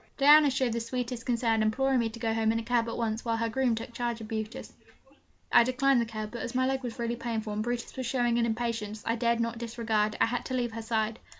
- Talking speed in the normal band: No, fast, 260 wpm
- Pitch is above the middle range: Yes, high, 235 Hz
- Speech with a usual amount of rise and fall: No, narrow, 1.5 semitones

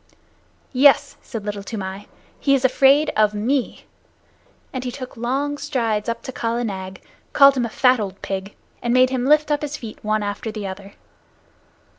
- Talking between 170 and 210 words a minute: Yes, average, 175 wpm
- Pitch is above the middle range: Yes, high, 240 Hz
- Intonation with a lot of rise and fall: No, average, 4.5 semitones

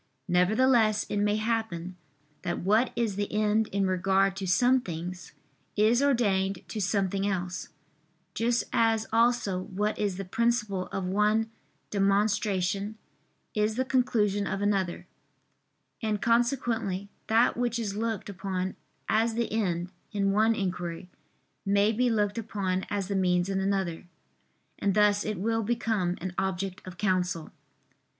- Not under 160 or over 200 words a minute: No, average, 140 wpm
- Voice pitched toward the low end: No, high, 205 Hz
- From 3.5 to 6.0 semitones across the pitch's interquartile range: No, average, 2.9 semitones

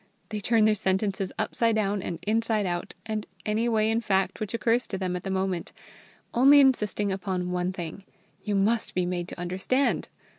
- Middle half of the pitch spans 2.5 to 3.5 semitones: Yes, average, 3.1 semitones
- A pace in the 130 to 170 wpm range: No, average, 185 wpm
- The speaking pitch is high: Yes, high, 200 Hz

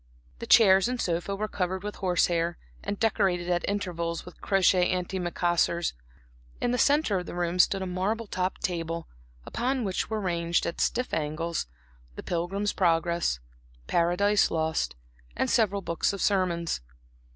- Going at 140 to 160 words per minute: Yes, average, 155 wpm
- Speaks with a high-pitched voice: No, medium, 180 Hz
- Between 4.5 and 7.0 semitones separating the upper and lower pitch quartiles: No, average, 2.9 semitones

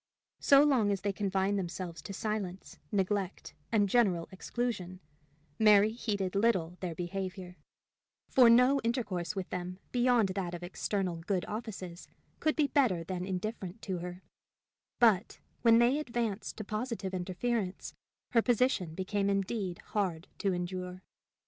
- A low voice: No, high, 195 Hz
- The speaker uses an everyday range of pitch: Yes, average, 3.9 semitones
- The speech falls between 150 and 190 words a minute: No, slow, 135 wpm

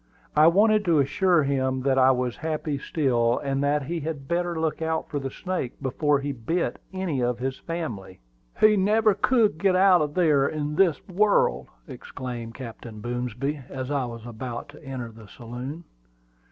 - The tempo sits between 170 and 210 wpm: Yes, average, 175 wpm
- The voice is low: No, medium, 145 Hz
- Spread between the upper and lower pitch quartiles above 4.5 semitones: Yes, average, 5.1 semitones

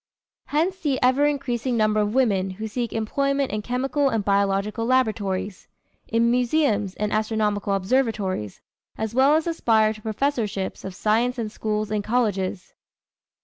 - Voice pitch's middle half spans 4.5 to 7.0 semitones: No, average, 3.8 semitones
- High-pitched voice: Yes, high, 220 Hz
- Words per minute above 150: No, average, 145 wpm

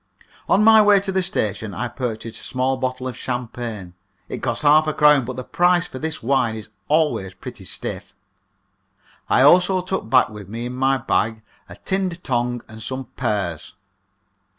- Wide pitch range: Yes, wide, 5.7 semitones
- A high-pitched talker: No, low, 130 Hz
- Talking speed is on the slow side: No, average, 175 wpm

